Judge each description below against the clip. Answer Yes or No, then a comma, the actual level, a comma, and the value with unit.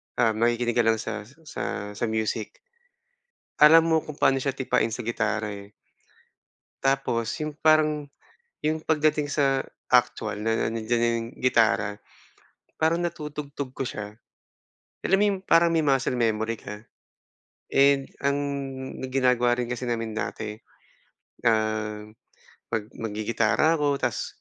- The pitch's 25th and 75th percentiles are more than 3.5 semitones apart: Yes, average, 4.6 semitones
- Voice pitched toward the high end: No, low, 120 Hz